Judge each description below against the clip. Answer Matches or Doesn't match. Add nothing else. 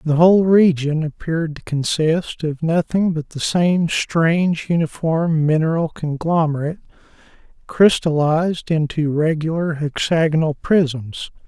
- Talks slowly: Matches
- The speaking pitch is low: Doesn't match